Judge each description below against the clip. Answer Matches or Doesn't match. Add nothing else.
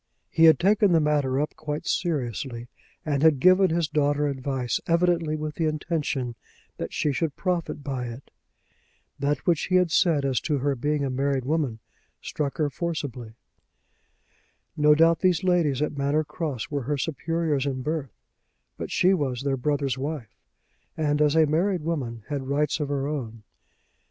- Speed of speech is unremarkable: Matches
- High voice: Doesn't match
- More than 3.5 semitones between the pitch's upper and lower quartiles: Doesn't match